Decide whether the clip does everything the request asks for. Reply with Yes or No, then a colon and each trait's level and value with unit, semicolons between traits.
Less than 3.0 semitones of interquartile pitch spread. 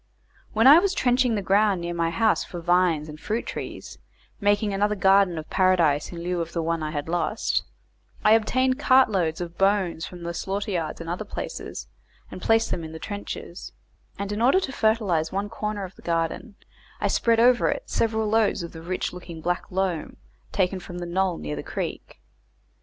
No: average, 4.2 semitones